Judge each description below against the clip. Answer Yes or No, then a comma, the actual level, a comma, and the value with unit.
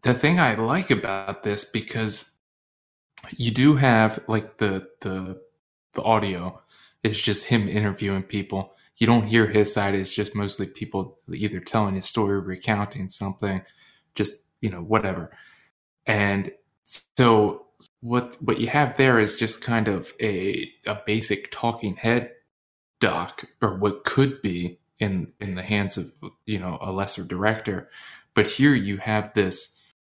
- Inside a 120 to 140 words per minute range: No, average, 150 wpm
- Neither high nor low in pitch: No, low, 105 Hz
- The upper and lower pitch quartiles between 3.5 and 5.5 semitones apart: No, average, 2.7 semitones